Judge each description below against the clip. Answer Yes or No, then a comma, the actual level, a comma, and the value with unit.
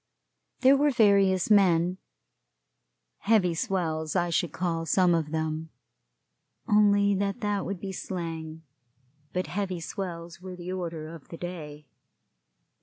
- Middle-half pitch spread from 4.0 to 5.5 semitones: No, average, 3.2 semitones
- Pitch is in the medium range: Yes, medium, 180 Hz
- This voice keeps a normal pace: No, slow, 125 wpm